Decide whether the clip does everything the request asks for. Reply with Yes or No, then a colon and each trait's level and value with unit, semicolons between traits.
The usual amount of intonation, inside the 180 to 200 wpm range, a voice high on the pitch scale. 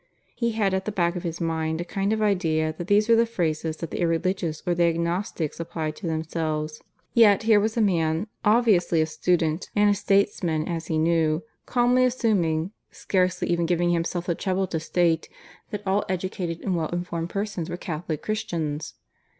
No: average, 3.6 semitones; average, 185 wpm; medium, 175 Hz